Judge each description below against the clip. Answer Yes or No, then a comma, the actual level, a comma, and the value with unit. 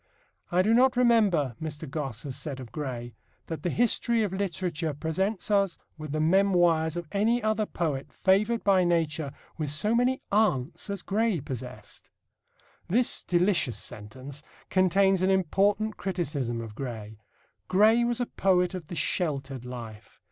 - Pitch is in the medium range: Yes, medium, 175 Hz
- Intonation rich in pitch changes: Yes, wide, 6.2 semitones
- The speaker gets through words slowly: No, average, 150 wpm